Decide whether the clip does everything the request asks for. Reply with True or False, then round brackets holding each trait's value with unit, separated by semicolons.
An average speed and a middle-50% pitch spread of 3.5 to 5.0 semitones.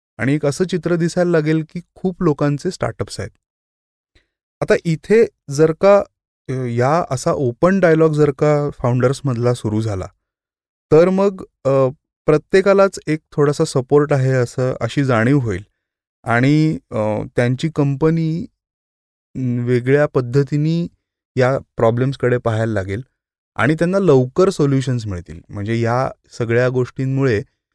True (115 wpm; 4.6 semitones)